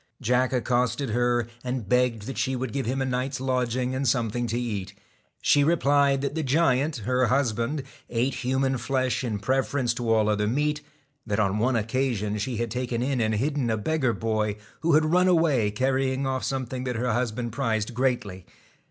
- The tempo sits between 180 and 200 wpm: Yes, average, 185 wpm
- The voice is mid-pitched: No, low, 125 Hz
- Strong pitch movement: No, average, 2.8 semitones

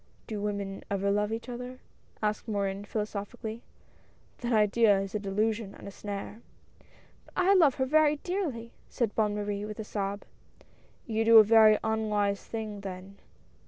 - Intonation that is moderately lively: No, narrow, 2.2 semitones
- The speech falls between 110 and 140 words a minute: No, average, 175 wpm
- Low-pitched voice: No, high, 215 Hz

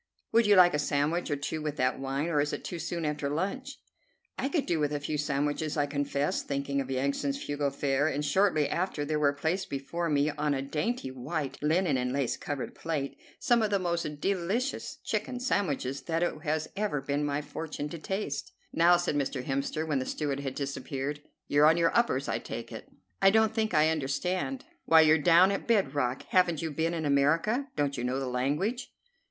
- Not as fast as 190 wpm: No, fast, 205 wpm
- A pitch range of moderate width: Yes, average, 3.8 semitones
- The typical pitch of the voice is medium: Yes, medium, 150 Hz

